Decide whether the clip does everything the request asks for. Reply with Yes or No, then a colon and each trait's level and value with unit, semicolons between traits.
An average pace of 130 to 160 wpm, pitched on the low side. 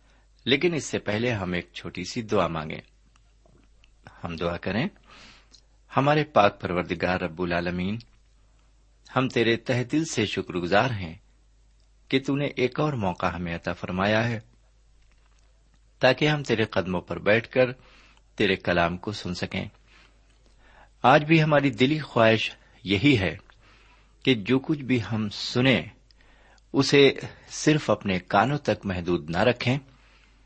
Yes: average, 135 wpm; low, 110 Hz